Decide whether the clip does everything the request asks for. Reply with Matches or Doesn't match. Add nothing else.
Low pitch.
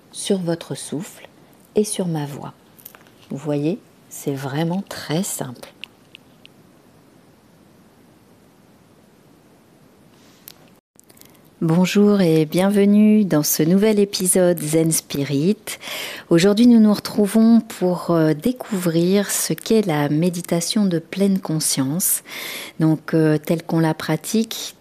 Doesn't match